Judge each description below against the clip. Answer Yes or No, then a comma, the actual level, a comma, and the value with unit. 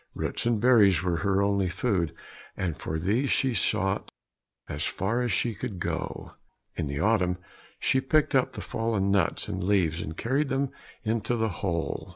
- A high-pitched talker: No, low, 100 Hz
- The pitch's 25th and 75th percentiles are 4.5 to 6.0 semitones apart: Yes, average, 4.8 semitones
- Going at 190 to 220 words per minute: No, average, 180 wpm